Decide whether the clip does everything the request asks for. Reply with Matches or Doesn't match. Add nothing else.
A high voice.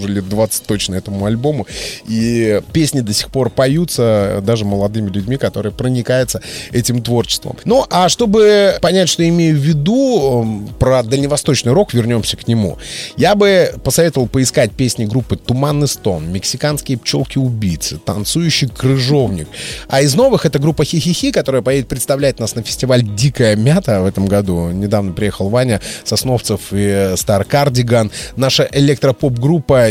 Doesn't match